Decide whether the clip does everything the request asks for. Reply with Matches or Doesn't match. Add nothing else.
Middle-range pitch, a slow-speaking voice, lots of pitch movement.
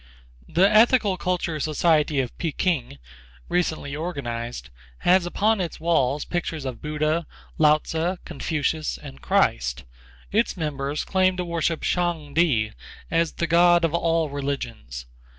Doesn't match